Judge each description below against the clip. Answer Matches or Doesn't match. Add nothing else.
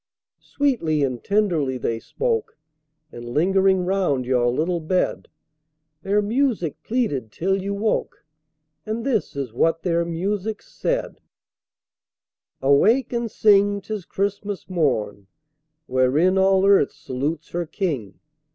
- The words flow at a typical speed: Doesn't match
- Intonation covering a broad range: Matches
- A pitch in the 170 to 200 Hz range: Matches